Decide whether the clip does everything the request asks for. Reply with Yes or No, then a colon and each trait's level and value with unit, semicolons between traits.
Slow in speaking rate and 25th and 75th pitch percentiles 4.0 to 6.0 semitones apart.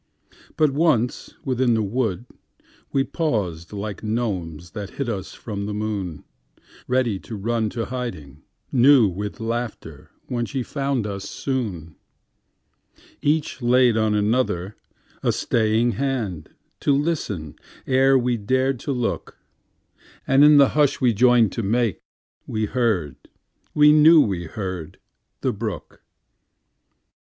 Yes: slow, 110 wpm; average, 4.5 semitones